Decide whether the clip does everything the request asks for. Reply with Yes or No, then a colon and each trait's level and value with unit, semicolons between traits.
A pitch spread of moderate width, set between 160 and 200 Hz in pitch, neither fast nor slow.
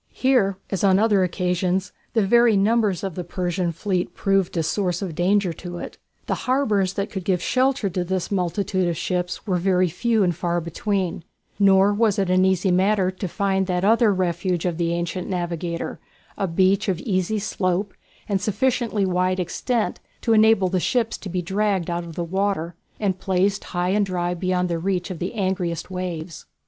No: narrow, 2.3 semitones; medium, 185 Hz; average, 185 wpm